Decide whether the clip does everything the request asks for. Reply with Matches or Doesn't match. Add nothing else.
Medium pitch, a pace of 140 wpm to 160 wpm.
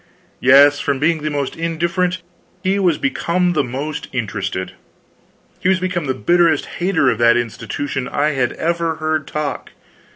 Matches